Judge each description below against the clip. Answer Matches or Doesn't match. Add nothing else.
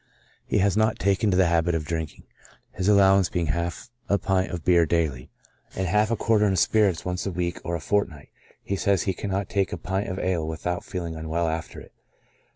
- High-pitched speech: Doesn't match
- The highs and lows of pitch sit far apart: Doesn't match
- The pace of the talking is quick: Matches